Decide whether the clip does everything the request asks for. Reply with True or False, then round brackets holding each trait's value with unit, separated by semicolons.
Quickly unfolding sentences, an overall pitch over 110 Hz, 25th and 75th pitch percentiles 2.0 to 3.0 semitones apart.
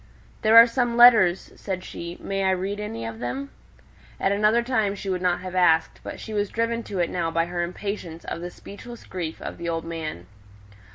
False (210 wpm; 185 Hz; 4.1 semitones)